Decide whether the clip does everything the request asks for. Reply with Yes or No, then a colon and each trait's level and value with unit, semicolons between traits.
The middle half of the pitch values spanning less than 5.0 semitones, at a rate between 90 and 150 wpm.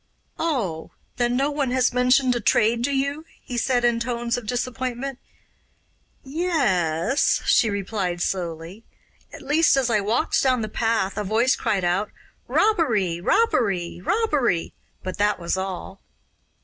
No: wide, 5.4 semitones; average, 145 wpm